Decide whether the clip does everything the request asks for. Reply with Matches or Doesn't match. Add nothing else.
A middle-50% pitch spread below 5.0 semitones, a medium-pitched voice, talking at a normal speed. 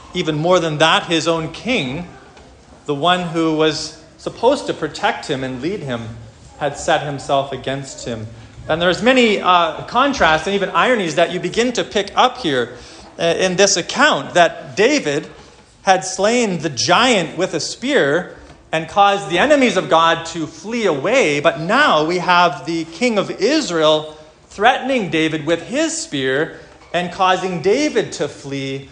Matches